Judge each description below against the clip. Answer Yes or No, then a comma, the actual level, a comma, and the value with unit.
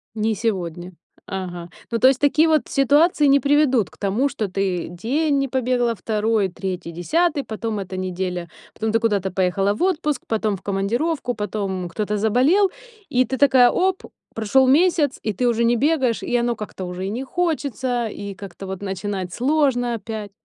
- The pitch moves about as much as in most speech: No, wide, 5.8 semitones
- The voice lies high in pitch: Yes, high, 225 Hz